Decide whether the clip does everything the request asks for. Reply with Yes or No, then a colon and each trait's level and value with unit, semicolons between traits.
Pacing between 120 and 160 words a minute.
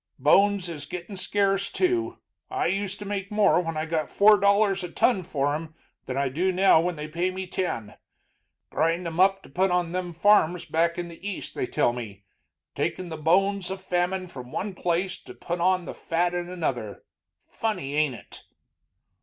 No: average, 185 wpm